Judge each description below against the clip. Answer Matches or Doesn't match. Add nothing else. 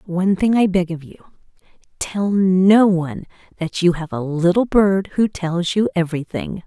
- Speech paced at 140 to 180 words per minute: Matches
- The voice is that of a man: Doesn't match